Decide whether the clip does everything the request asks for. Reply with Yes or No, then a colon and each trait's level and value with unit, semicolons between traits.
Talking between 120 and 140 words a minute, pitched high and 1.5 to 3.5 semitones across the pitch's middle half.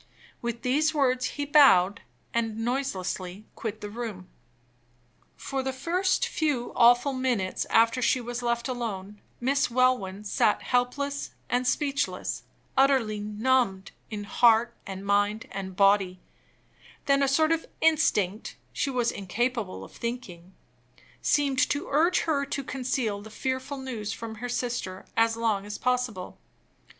No: slow, 135 wpm; high, 240 Hz; average, 4.3 semitones